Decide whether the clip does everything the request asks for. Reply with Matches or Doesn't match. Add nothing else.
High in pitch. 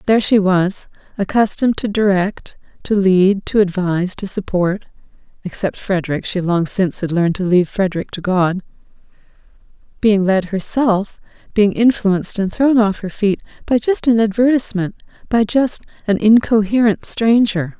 Matches